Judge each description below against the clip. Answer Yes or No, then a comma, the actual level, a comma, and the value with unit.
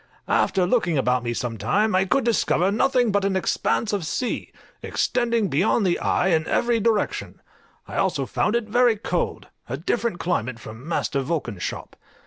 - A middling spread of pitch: No, wide, 6.8 semitones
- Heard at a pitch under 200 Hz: Yes, high, 190 Hz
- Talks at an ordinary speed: Yes, average, 170 wpm